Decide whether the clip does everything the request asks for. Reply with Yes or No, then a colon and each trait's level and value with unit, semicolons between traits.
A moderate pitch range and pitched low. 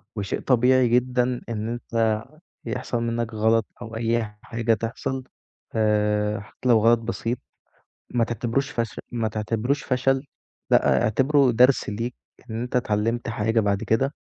No: narrow, 2.1 semitones; low, 115 Hz